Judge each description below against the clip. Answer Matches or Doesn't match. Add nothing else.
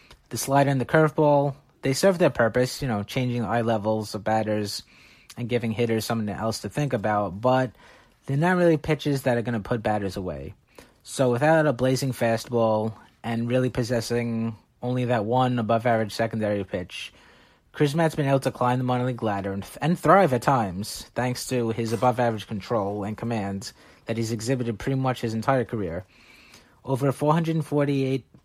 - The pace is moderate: Matches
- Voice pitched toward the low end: Matches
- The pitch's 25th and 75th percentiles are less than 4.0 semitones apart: Matches